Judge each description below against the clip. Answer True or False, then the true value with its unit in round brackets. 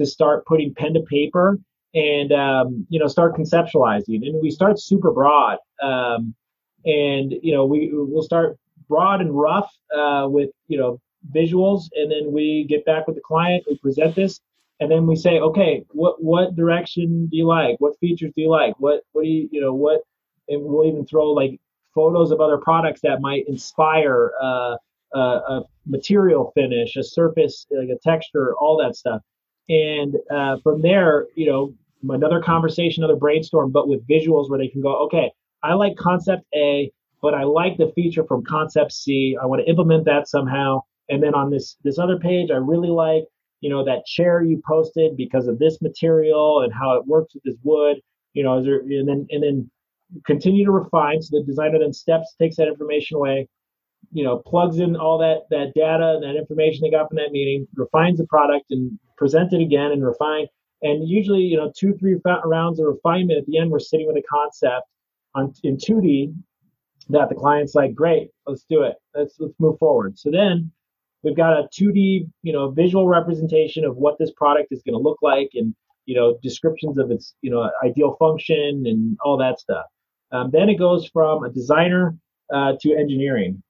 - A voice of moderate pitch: True (155 Hz)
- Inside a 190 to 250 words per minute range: True (195 wpm)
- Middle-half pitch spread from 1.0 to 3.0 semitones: True (2.5 semitones)